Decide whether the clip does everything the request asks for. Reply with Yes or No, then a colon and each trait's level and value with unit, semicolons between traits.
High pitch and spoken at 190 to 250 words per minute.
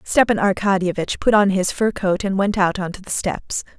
Yes: high, 195 Hz; fast, 205 wpm